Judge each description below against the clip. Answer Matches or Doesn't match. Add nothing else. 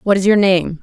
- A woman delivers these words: Matches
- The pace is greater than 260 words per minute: Matches